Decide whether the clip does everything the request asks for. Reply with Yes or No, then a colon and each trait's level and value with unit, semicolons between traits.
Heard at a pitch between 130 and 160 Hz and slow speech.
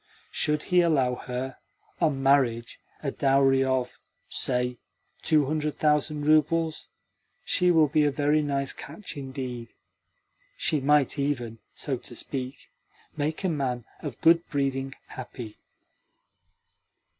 Yes: medium, 140 Hz; slow, 120 wpm